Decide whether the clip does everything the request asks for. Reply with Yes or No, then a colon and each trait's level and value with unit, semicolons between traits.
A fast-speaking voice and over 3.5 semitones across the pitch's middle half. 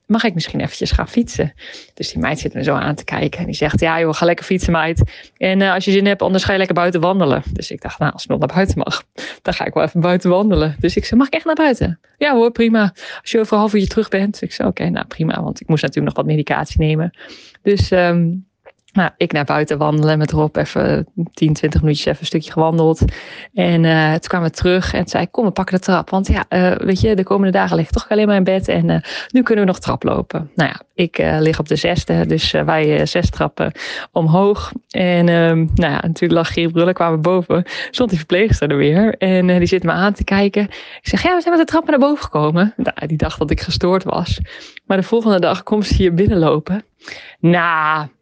Yes: fast, 255 wpm; average, 4.0 semitones